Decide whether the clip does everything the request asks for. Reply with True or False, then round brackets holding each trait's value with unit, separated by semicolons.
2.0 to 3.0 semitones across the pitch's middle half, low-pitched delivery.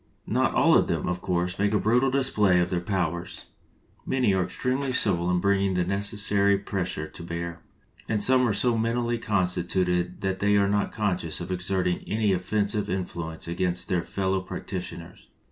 True (2.6 semitones; 95 Hz)